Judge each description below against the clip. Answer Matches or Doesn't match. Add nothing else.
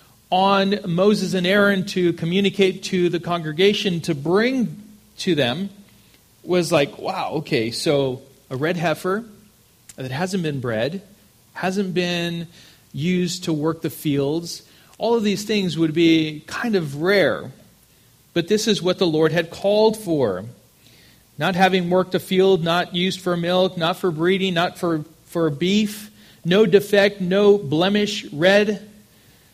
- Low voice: Doesn't match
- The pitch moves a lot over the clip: Doesn't match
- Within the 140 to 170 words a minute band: Matches